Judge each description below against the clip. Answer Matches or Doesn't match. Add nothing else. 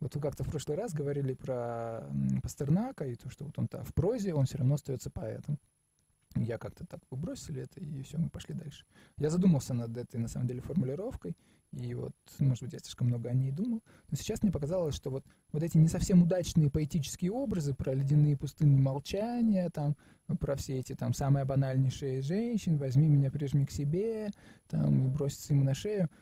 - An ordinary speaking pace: Doesn't match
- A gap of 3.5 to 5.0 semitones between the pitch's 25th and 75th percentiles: Matches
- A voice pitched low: Doesn't match